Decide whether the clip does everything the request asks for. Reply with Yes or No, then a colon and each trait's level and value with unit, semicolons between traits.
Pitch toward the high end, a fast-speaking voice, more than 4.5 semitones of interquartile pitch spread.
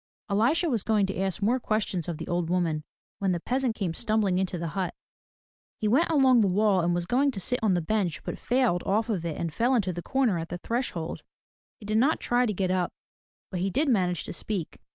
Yes: high, 200 Hz; fast, 230 wpm; average, 5.0 semitones